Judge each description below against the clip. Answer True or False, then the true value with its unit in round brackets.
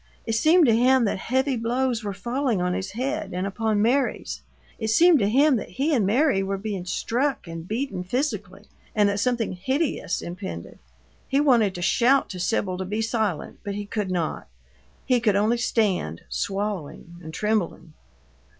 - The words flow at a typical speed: True (175 wpm)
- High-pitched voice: True (215 Hz)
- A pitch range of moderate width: True (4.8 semitones)